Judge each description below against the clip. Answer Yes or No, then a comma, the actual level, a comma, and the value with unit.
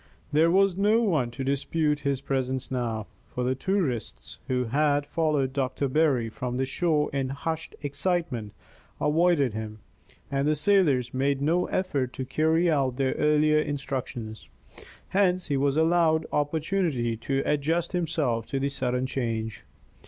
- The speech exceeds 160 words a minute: No, average, 145 wpm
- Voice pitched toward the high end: No, medium, 140 Hz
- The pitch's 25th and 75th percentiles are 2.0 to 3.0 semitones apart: No, average, 3.8 semitones